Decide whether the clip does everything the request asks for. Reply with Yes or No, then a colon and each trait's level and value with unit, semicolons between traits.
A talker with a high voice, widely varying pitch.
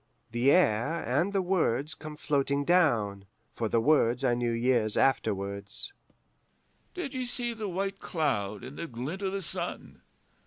No: medium, 140 Hz; wide, 7.8 semitones